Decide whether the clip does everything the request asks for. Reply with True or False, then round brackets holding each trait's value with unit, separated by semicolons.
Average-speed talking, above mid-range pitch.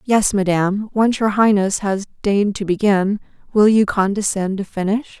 True (160 wpm; 205 Hz)